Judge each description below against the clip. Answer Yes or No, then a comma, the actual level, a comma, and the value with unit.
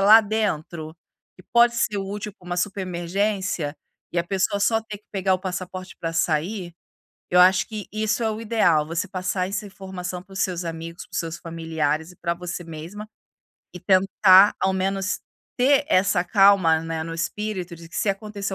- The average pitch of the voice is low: No, medium, 185 Hz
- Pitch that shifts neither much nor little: Yes, average, 3.1 semitones